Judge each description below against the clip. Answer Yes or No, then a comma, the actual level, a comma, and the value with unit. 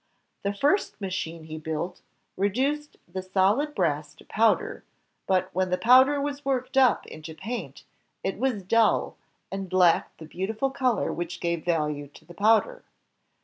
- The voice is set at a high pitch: Yes, high, 195 Hz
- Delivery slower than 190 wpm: Yes, average, 155 wpm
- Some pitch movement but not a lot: No, wide, 6.8 semitones